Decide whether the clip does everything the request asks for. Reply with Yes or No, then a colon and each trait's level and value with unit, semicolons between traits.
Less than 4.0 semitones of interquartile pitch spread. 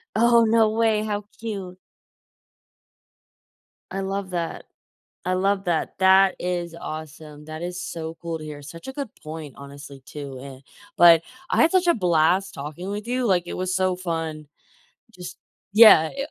No: average, 4.3 semitones